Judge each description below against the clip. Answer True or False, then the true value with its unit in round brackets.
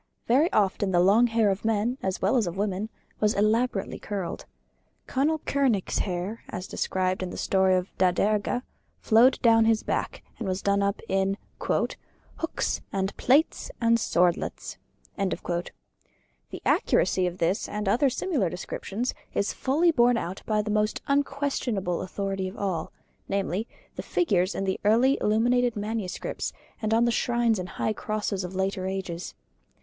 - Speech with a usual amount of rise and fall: True (3.7 semitones)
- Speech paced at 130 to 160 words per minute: True (155 wpm)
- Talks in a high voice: True (205 Hz)